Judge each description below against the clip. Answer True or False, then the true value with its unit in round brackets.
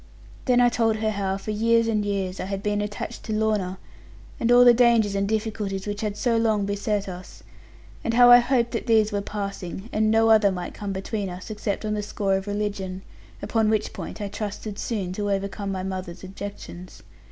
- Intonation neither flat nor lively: False (2.1 semitones)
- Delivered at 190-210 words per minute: True (205 wpm)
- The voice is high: True (205 Hz)